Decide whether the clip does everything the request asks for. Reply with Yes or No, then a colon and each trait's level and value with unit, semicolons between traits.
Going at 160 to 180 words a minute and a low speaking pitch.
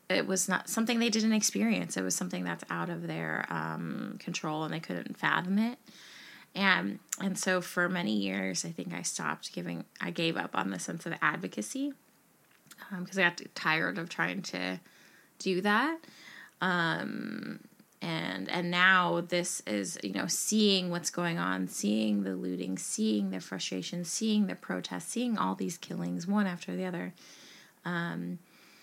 No: average, 165 wpm; medium, 175 Hz